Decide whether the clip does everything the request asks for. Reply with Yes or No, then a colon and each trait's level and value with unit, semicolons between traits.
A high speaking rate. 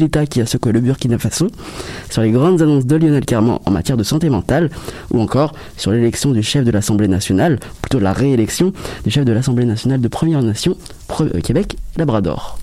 No: average, 200 wpm